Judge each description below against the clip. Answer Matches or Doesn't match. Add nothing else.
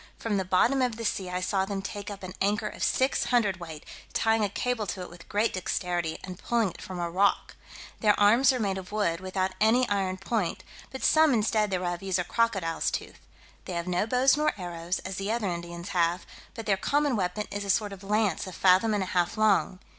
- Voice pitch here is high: Matches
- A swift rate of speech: Matches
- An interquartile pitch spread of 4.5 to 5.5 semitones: Doesn't match